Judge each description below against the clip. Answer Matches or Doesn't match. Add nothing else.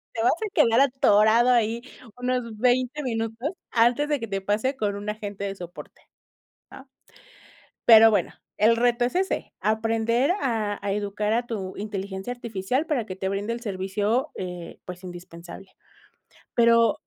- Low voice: Doesn't match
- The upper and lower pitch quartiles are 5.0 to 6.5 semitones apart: Doesn't match